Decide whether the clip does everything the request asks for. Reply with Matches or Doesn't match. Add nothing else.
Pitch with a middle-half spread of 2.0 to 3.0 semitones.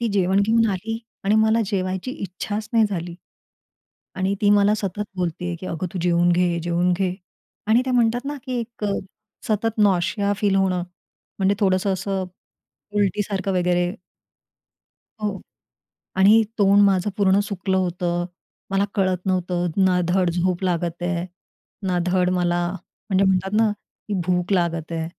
Matches